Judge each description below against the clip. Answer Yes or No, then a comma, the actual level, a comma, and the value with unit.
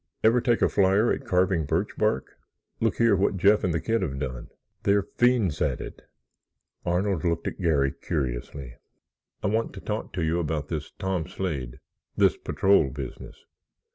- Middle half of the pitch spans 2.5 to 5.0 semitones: No, wide, 5.5 semitones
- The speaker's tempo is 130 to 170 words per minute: Yes, average, 160 wpm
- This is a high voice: No, very low, 90 Hz